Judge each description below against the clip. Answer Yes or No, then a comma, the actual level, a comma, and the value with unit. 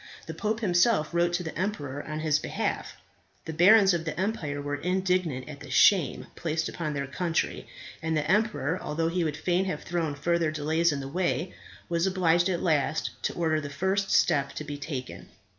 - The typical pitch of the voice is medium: Yes, medium, 165 Hz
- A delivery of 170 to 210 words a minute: Yes, average, 195 wpm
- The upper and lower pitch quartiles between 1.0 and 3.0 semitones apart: No, average, 3.4 semitones